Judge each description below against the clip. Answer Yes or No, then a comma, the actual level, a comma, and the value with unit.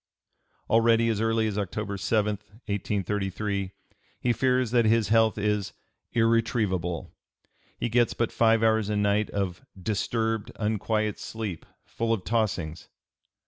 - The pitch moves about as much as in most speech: No, narrow, 2.0 semitones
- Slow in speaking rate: Yes, slow, 125 wpm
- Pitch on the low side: Yes, low, 110 Hz